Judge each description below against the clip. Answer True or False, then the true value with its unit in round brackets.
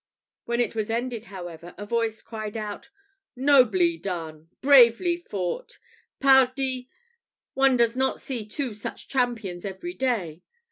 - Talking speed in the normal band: False (130 wpm)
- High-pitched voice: True (230 Hz)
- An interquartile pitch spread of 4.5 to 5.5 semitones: True (4.9 semitones)